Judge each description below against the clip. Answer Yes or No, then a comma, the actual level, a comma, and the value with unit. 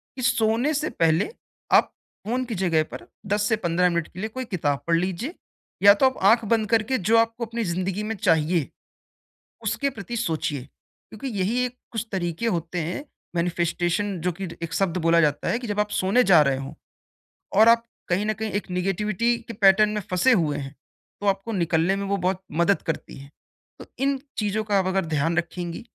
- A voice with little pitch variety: No, average, 4.8 semitones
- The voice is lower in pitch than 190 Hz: No, high, 195 Hz